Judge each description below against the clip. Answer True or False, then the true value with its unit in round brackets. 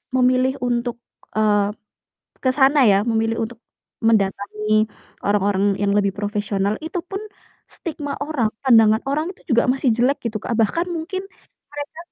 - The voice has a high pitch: True (230 Hz)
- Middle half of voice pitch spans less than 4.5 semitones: False (5.1 semitones)